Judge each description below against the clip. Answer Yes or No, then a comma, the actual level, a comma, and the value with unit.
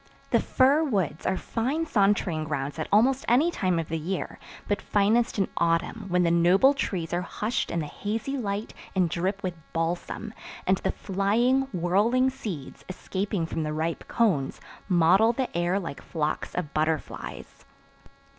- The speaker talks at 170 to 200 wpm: No, average, 160 wpm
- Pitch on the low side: No, high, 190 Hz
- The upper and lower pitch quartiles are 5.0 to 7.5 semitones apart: Yes, average, 5.3 semitones